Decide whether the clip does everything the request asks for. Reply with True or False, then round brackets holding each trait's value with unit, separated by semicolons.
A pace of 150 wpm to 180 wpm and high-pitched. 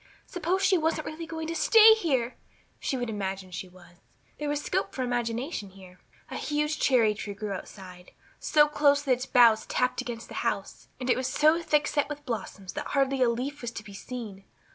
False (205 wpm; 255 Hz)